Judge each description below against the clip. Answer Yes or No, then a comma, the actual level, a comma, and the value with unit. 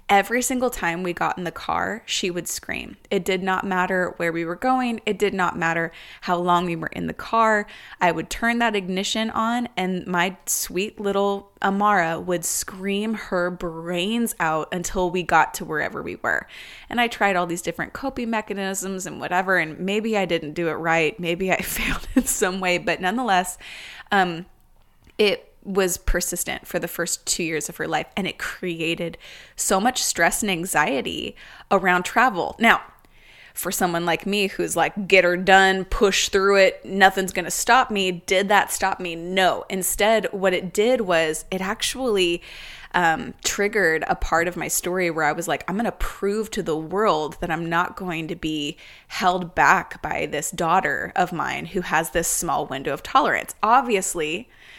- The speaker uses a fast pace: No, average, 185 wpm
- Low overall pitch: No, medium, 185 Hz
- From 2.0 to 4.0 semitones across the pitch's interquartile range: Yes, average, 2.9 semitones